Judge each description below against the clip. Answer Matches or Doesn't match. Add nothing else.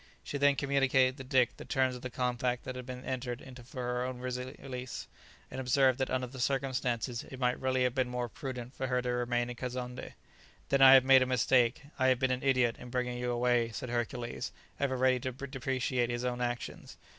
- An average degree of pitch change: Doesn't match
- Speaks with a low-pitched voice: Matches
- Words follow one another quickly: Matches